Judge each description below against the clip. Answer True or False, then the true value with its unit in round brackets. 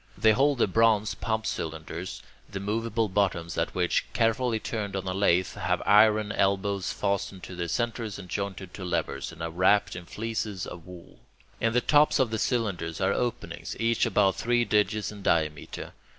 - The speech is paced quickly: False (180 wpm)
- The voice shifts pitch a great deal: False (3.6 semitones)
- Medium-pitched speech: False (100 Hz)